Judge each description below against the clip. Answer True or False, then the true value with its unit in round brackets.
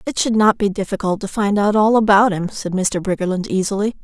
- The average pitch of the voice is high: True (205 Hz)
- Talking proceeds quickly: True (225 wpm)